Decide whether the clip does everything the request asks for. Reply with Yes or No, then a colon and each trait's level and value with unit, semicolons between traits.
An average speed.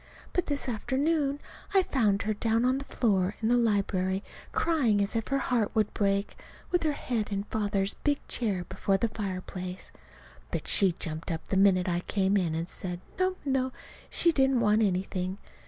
Yes: average, 180 wpm